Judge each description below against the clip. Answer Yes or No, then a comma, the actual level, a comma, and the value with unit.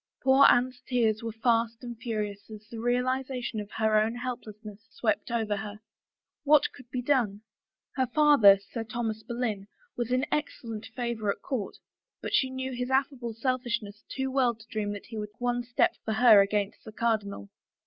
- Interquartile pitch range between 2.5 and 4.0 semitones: Yes, average, 2.8 semitones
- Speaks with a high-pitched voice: Yes, high, 230 Hz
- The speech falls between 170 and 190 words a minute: Yes, average, 185 wpm